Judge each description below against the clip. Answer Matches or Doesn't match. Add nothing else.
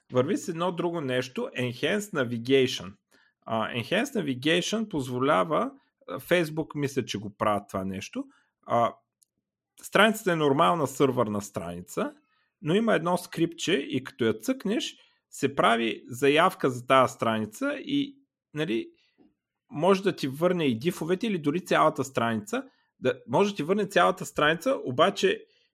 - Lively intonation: Matches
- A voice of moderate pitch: Matches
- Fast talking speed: Doesn't match